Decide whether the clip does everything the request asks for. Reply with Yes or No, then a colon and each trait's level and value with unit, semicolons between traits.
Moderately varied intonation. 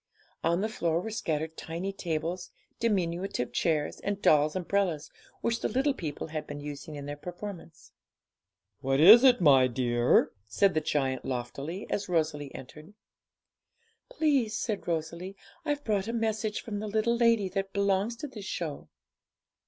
No: wide, 5.9 semitones